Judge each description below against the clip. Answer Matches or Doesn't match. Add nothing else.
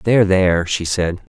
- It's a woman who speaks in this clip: Doesn't match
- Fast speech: Doesn't match